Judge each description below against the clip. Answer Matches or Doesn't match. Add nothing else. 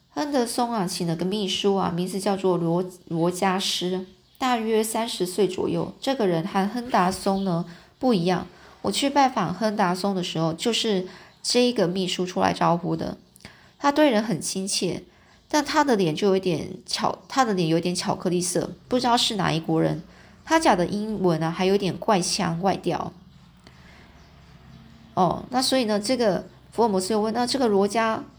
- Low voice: Doesn't match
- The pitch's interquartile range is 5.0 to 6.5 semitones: Doesn't match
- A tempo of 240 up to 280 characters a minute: Matches